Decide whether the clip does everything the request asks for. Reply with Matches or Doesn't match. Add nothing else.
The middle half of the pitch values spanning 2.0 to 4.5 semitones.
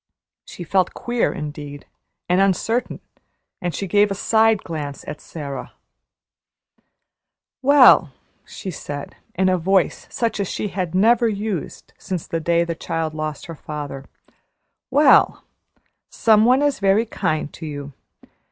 Doesn't match